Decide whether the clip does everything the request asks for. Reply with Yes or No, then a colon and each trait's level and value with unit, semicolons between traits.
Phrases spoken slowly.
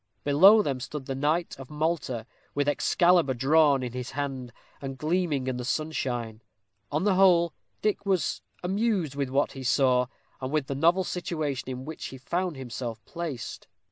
No: average, 170 wpm